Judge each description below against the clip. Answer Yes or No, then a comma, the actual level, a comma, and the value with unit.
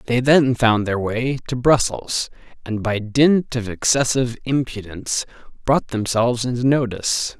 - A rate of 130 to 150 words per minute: Yes, average, 140 wpm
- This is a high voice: No, low, 120 Hz